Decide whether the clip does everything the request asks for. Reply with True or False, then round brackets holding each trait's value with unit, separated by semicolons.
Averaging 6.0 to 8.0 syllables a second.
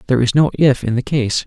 True (6.6 syllables/s)